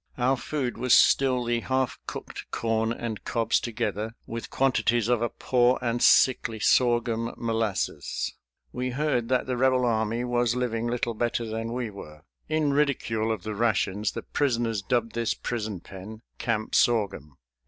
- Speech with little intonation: Yes, narrow, 2.0 semitones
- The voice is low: Yes, low, 115 Hz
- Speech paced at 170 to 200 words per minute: No, average, 155 wpm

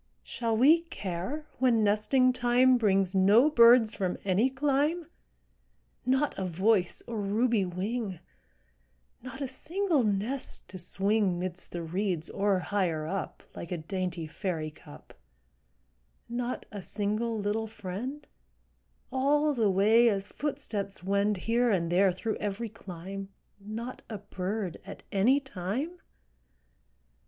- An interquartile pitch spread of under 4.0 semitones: No, average, 4.7 semitones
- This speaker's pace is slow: Yes, slow, 130 wpm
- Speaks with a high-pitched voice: Yes, high, 210 Hz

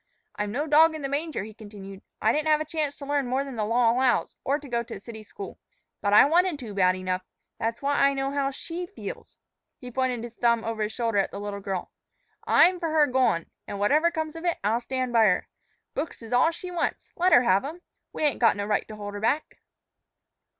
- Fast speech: Yes, fast, 240 wpm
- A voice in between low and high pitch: No, very high, 250 Hz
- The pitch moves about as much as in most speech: No, wide, 5.9 semitones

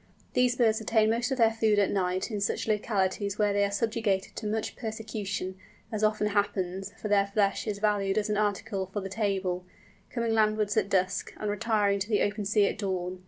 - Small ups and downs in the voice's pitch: Yes, narrow, 1.7 semitones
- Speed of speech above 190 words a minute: Yes, fast, 205 wpm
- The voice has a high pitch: Yes, high, 205 Hz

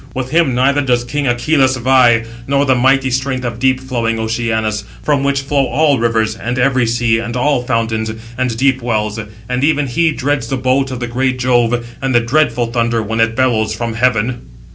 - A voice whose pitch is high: No, low, 125 Hz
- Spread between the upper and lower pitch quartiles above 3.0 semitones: No, narrow, 2.5 semitones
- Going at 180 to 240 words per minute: Yes, average, 195 wpm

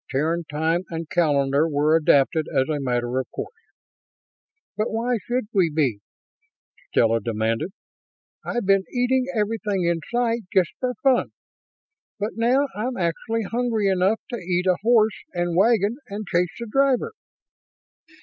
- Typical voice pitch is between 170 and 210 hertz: Yes, high, 190 Hz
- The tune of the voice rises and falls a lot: Yes, wide, 6.5 semitones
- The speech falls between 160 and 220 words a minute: No, average, 140 wpm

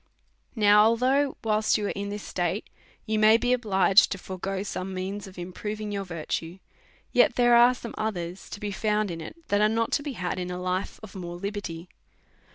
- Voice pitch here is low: No, high, 205 Hz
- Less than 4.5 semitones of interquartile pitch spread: Yes, average, 2.9 semitones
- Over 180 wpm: Yes, average, 200 wpm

